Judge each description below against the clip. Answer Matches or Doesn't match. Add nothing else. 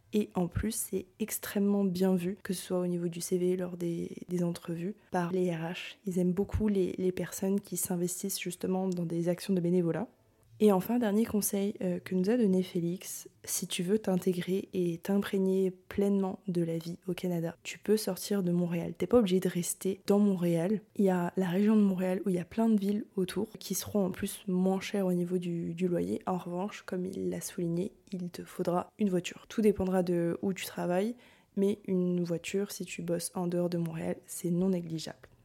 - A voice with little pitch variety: Matches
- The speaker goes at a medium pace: Matches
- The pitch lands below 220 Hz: Matches